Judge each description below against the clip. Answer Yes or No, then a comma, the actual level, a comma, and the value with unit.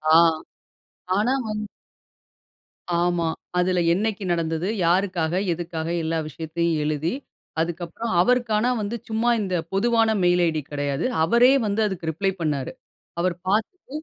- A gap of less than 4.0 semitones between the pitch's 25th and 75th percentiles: No, average, 4.5 semitones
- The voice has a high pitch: No, medium, 180 Hz